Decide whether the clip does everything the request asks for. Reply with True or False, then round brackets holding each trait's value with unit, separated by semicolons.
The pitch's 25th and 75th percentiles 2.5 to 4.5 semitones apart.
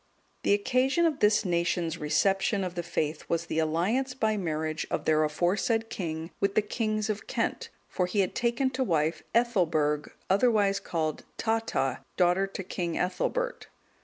False (5.3 semitones)